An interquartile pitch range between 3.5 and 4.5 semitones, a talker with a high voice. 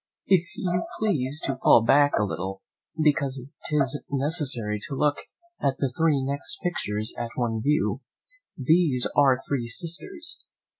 No: average, 4.2 semitones; medium, 140 Hz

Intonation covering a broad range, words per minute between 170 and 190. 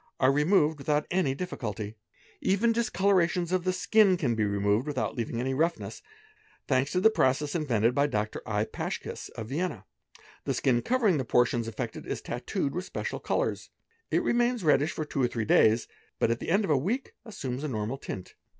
Yes: wide, 7.6 semitones; average, 185 wpm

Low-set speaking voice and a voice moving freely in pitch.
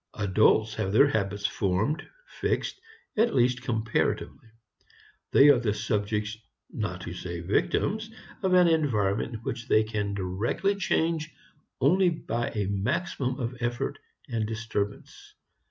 Yes: low, 115 Hz; wide, 5.7 semitones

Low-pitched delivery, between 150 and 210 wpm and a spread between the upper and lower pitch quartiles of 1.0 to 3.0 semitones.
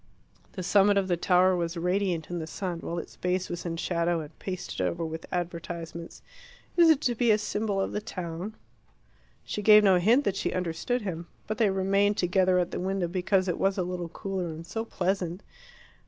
No: medium, 185 Hz; average, 200 wpm; narrow, 2.6 semitones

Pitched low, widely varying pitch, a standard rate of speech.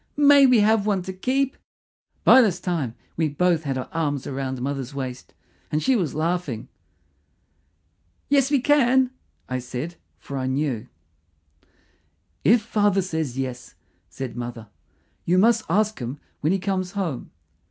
No: medium, 170 Hz; wide, 7.9 semitones; average, 145 wpm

